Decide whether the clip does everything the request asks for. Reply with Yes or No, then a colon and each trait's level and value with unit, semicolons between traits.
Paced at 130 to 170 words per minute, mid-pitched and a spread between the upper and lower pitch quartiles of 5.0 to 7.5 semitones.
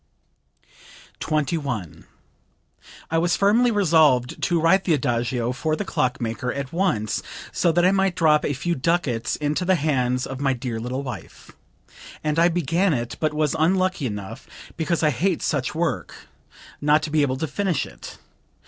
Yes: average, 165 wpm; medium, 150 Hz; average, 5.3 semitones